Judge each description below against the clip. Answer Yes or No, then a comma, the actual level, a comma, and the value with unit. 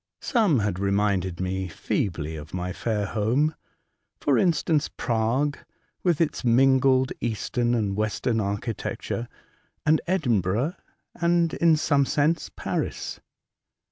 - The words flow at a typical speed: No, slow, 115 wpm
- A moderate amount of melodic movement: No, wide, 6.9 semitones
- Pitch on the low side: Yes, low, 120 Hz